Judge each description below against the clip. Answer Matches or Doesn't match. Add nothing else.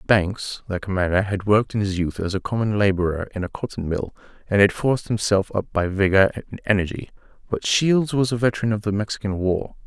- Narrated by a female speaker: Doesn't match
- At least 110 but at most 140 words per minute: Doesn't match